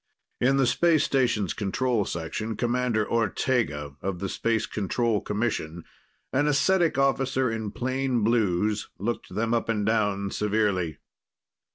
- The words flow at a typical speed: No, slow, 130 wpm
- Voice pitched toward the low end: Yes, low, 115 Hz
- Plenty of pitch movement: No, average, 3.8 semitones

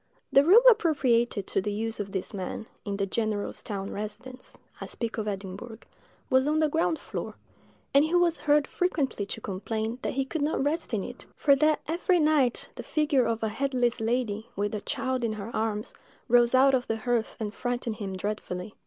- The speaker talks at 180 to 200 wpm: Yes, average, 195 wpm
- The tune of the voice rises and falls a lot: No, average, 4.9 semitones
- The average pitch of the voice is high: Yes, high, 235 Hz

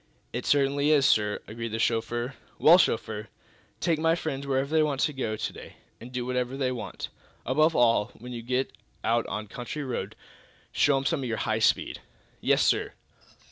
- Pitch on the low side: Yes, low, 125 Hz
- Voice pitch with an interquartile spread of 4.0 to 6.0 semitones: No, average, 3.6 semitones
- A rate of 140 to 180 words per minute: No, average, 190 wpm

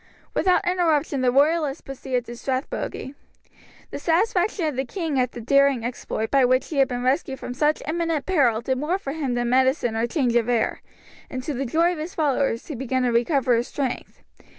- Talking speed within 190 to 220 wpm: Yes, average, 200 wpm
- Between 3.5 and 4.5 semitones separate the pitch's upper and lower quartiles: Yes, average, 3.9 semitones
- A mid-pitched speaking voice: No, very high, 270 Hz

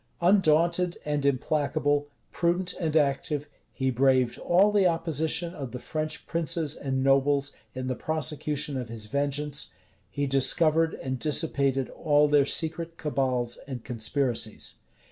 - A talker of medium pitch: Yes, medium, 145 Hz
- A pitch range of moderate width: Yes, average, 3.3 semitones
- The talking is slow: Yes, slow, 130 wpm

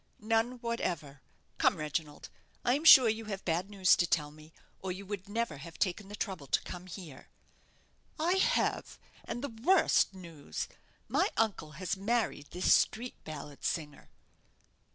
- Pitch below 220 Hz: Yes, high, 190 Hz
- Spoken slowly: No, average, 155 wpm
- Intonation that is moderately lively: No, wide, 6.1 semitones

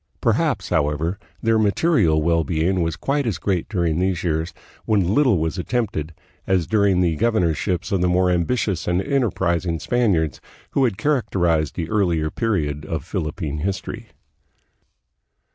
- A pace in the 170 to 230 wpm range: No, average, 145 wpm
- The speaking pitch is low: Yes, very low, 90 Hz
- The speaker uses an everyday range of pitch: Yes, average, 4.5 semitones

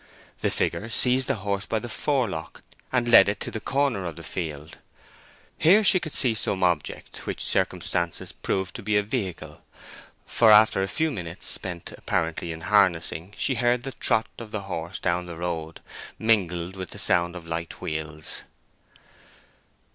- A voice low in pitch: Yes, very low, 95 Hz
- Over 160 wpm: Yes, average, 170 wpm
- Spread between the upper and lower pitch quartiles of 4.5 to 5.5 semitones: Yes, average, 5.1 semitones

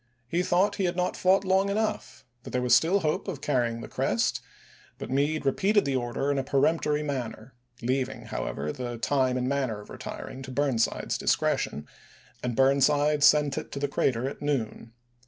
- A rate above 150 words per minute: Yes, average, 195 wpm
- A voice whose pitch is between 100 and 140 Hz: Yes, low, 135 Hz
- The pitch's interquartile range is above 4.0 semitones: No, average, 3.3 semitones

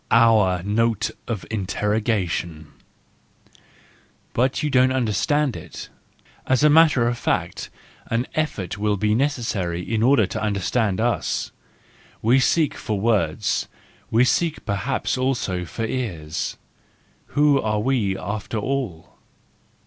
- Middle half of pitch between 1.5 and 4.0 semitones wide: No, average, 4.5 semitones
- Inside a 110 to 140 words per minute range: Yes, slow, 135 wpm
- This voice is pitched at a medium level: No, low, 110 Hz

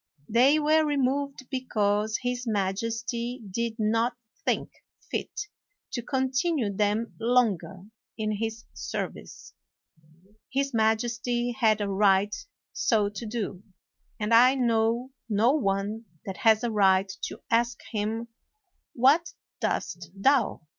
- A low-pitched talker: No, high, 230 Hz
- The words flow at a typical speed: No, slow, 115 wpm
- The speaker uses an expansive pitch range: No, average, 3.2 semitones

